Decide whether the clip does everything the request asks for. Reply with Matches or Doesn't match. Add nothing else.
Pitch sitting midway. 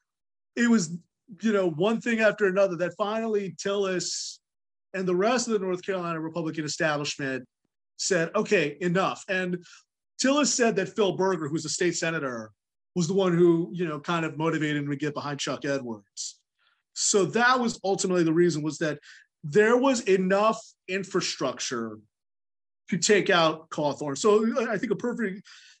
Matches